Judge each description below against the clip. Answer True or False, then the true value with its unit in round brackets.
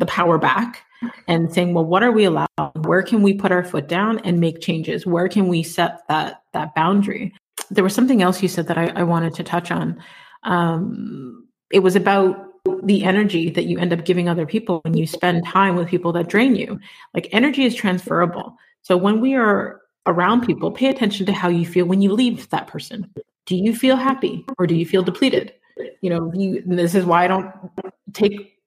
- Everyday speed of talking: False (210 wpm)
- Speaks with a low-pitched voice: False (185 Hz)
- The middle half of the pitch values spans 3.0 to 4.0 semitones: True (3.5 semitones)